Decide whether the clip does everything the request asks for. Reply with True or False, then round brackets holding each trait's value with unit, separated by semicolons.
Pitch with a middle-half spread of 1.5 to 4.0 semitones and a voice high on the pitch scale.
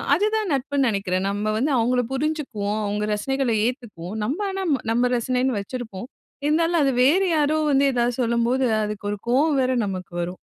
False (5.2 semitones; 250 Hz)